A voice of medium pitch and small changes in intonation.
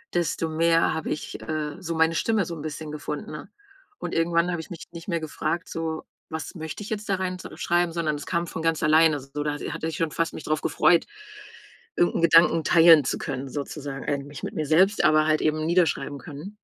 Yes: medium, 160 Hz; narrow, 1.8 semitones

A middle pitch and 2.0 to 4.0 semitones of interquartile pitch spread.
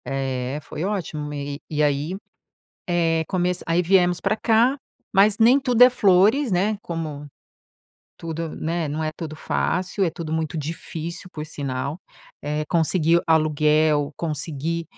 Yes: medium, 165 Hz; average, 3.3 semitones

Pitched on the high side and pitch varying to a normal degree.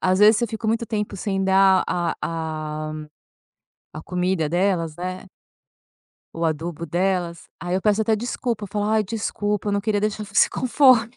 Yes: high, 195 Hz; average, 3.6 semitones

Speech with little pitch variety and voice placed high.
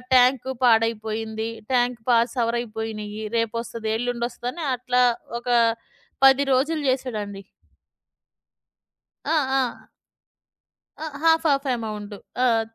Yes: narrow, 2.2 semitones; high, 235 Hz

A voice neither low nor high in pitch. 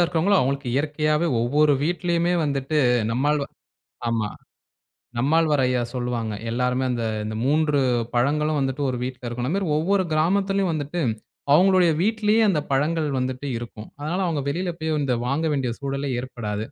Yes: medium, 145 Hz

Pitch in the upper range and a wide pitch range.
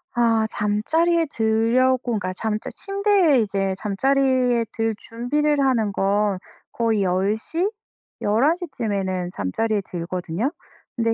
No: high, 225 Hz; average, 4.6 semitones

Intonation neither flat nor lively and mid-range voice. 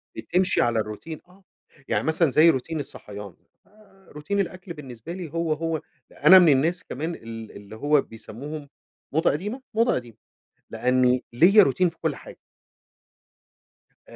No: wide, 5.7 semitones; medium, 155 Hz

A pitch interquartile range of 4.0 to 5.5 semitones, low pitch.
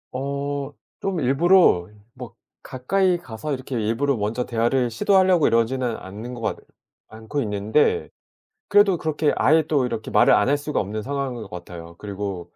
Yes: average, 5.2 semitones; low, 130 Hz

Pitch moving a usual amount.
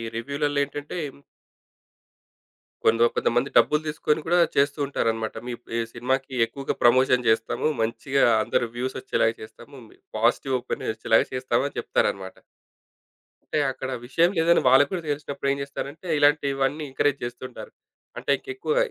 Yes: average, 3.3 semitones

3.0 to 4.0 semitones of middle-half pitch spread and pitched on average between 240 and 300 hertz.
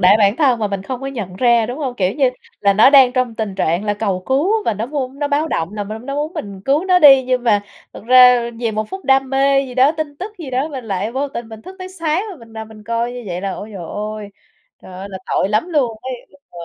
No: average, 4.8 semitones; high, 245 Hz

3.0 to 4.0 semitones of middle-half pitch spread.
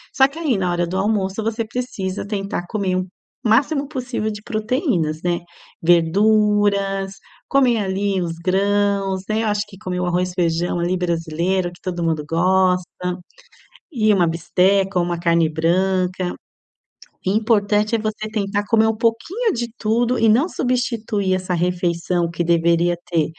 Yes: average, 3.6 semitones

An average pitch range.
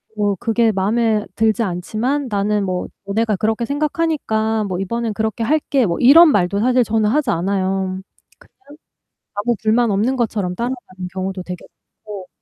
Yes: average, 3.6 semitones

